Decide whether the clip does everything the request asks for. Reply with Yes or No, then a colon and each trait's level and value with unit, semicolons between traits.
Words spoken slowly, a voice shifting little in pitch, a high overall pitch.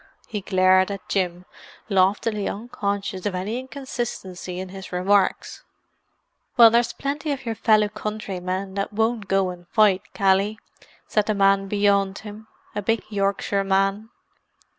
Yes: slow, 130 wpm; narrow, 2.2 semitones; high, 200 Hz